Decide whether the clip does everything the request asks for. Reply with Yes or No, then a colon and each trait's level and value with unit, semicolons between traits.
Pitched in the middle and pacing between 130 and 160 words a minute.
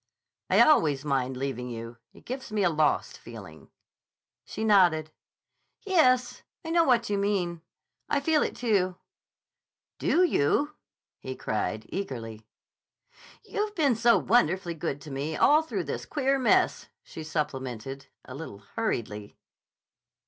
Yes: medium, 165 Hz; slow, 135 wpm